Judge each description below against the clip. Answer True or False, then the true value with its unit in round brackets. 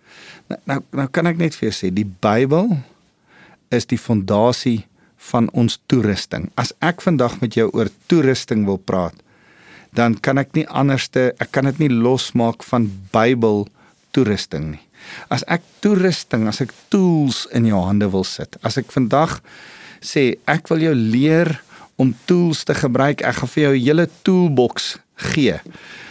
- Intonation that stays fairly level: False (5.3 semitones)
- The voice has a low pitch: True (125 Hz)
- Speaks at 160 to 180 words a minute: True (165 wpm)